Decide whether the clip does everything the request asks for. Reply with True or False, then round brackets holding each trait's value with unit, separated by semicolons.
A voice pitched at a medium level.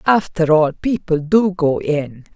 True (175 Hz)